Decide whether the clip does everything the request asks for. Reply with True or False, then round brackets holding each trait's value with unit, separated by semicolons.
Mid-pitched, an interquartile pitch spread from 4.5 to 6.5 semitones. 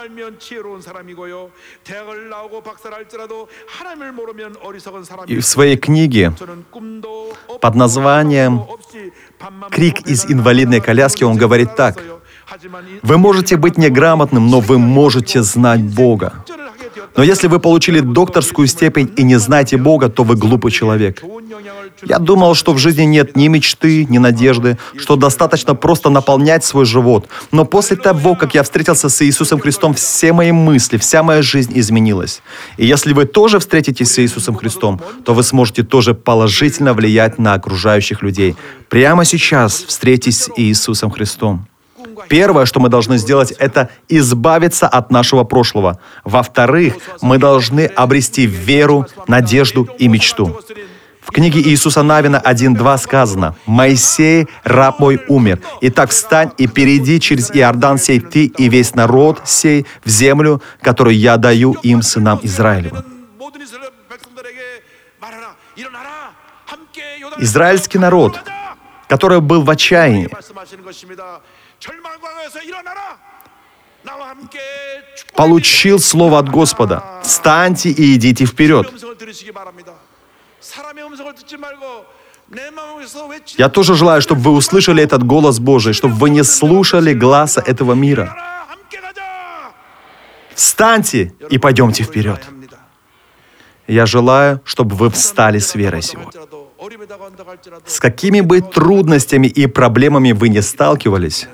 False (145 Hz; 7.4 semitones)